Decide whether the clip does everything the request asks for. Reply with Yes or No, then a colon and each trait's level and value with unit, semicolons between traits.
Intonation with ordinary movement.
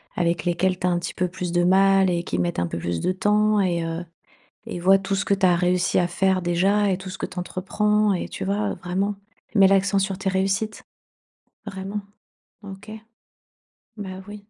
No: narrow, 2.0 semitones